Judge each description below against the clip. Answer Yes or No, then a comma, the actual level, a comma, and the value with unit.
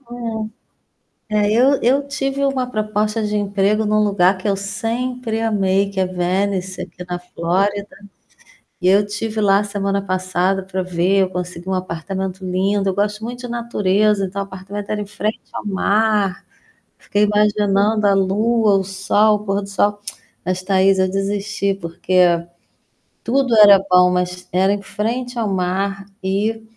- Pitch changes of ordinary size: No, narrow, 2.1 semitones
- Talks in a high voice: Yes, high, 200 Hz